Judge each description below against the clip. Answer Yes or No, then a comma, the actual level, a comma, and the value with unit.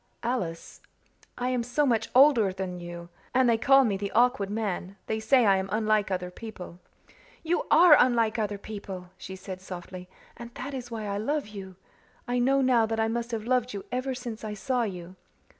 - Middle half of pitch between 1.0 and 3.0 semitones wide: No, average, 4.4 semitones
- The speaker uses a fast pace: No, average, 195 wpm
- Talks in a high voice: Yes, high, 220 Hz